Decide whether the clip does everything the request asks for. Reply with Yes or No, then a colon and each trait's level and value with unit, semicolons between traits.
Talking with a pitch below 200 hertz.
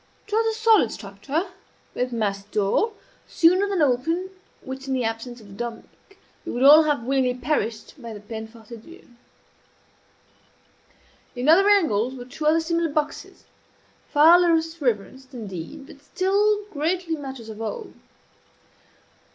No: very high, 275 Hz